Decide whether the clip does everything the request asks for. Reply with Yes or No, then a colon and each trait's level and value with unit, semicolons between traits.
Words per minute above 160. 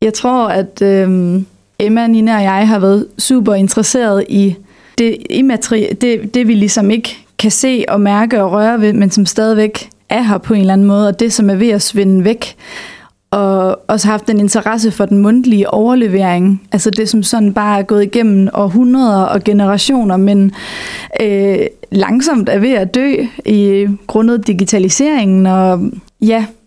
Yes: average, 175 wpm